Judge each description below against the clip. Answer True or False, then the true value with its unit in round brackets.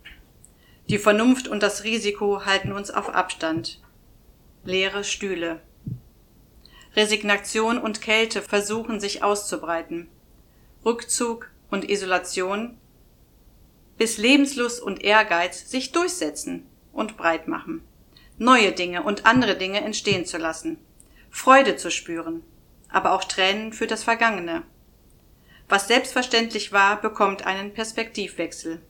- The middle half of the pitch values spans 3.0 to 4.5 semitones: True (3.6 semitones)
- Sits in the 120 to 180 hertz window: False (205 Hz)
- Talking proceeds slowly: True (110 wpm)